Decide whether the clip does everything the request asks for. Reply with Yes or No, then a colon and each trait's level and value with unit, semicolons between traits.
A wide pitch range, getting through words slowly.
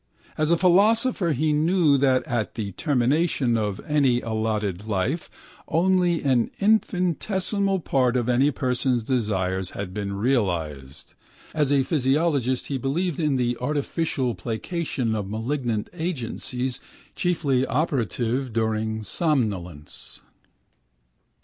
Yes: wide, 6.2 semitones; slow, 110 wpm